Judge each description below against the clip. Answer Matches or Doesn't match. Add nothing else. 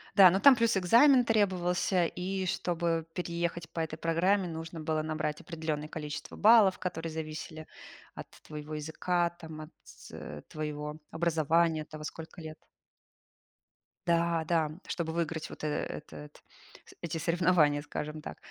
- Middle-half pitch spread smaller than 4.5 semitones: Matches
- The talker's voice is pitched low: Doesn't match